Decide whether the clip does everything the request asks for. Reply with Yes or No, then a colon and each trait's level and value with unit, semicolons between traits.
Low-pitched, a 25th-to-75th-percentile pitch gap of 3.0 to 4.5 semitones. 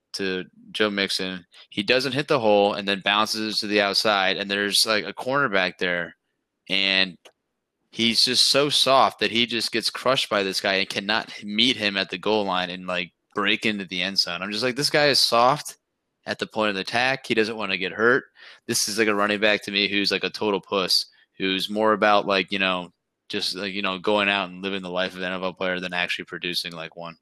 No: low, 100 Hz; narrow, 2.5 semitones